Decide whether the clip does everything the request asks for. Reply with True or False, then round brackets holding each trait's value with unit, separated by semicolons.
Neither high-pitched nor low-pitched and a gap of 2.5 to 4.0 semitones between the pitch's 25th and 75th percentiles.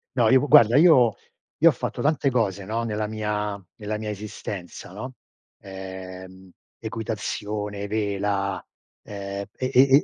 False (105 Hz; 2.8 semitones)